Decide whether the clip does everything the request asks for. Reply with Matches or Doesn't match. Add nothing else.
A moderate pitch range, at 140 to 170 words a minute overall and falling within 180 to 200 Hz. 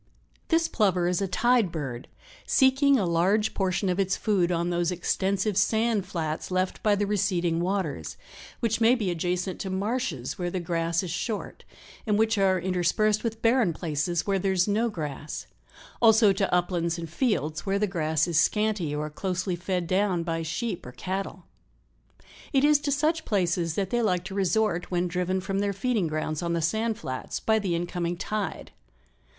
Doesn't match